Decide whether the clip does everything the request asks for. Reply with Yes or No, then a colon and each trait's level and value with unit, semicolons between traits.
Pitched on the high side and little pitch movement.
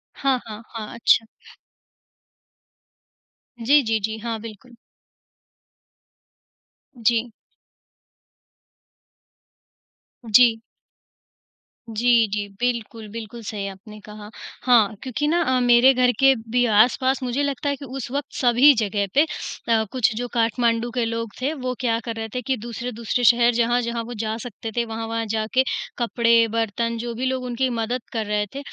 Yes: high, 235 Hz; narrow, 2.0 semitones